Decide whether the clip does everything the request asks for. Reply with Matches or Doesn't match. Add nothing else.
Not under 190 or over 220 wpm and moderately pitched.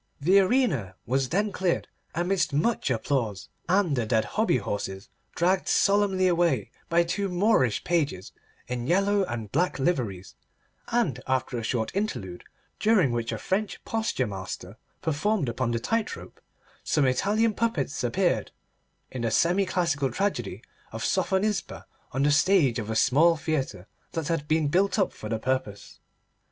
Doesn't match